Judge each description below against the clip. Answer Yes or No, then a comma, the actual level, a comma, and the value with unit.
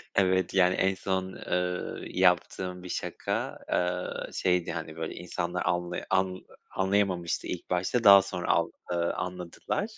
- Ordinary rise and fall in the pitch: No, narrow, 1.1 semitones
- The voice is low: Yes, very low, 90 Hz